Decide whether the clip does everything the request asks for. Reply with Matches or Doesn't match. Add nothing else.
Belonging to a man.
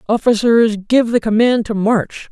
Matches